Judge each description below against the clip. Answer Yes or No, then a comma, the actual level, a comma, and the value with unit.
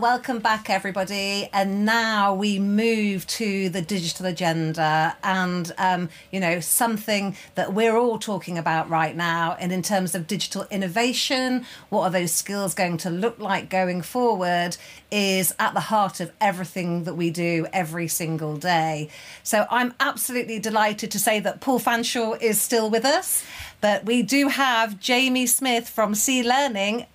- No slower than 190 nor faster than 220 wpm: No, average, 160 wpm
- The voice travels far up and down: No, average, 4.2 semitones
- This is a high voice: Yes, high, 200 Hz